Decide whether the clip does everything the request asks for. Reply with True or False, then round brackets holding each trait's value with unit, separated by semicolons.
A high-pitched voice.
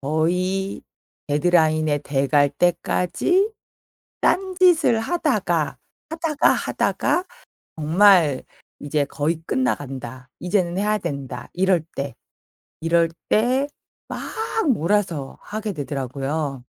False (170 Hz)